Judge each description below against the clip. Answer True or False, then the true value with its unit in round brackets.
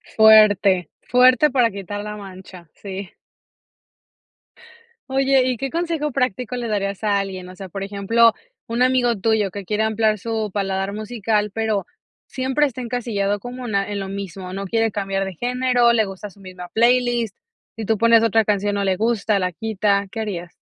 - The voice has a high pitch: True (210 Hz)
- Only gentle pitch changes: False (3.2 semitones)